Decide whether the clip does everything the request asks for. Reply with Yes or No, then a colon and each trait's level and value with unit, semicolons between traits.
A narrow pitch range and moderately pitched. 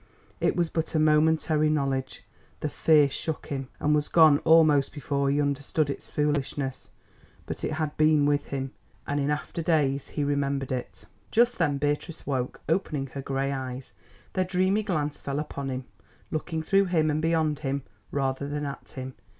Yes: narrow, 2.3 semitones; medium, 145 Hz